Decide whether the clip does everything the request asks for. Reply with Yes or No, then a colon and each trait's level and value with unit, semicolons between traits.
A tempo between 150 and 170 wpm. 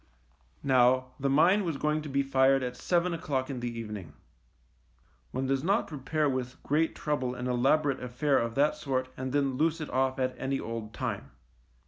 No: average, 185 wpm